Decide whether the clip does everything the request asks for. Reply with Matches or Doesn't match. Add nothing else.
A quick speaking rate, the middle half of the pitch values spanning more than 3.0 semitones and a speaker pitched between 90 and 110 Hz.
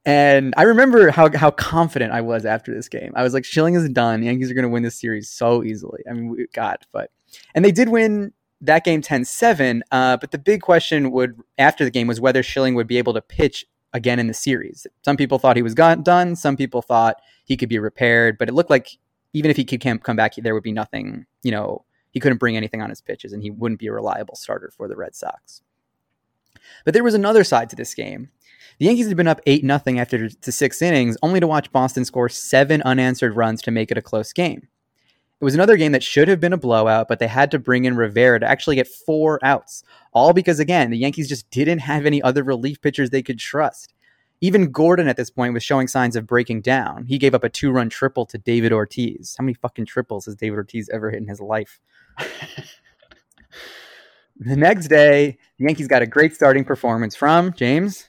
Doesn't match